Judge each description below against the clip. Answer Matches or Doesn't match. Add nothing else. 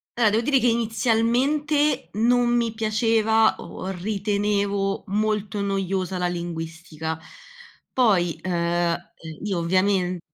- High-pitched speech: Matches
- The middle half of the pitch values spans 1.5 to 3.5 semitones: Doesn't match